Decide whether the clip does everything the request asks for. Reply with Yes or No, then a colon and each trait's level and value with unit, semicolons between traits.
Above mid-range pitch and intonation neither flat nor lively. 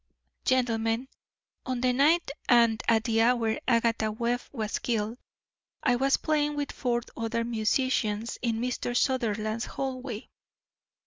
No: high, 240 Hz; narrow, 2.3 semitones